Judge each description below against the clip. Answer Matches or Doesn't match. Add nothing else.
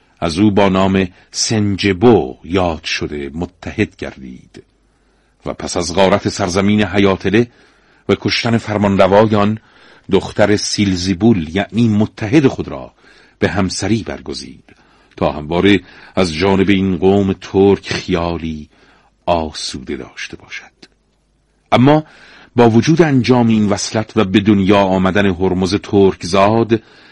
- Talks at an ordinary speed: Matches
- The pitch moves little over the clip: Matches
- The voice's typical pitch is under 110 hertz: Matches